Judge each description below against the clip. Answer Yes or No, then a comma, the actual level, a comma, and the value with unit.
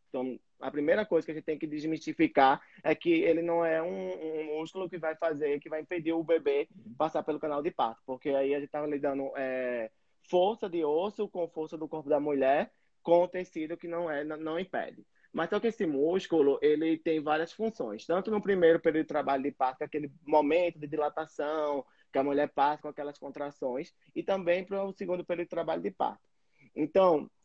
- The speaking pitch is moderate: Yes, medium, 155 Hz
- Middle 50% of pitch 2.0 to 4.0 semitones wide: Yes, average, 2.9 semitones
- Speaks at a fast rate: Yes, fast, 215 wpm